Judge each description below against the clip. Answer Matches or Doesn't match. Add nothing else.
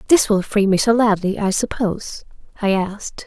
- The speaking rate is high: Doesn't match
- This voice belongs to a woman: Matches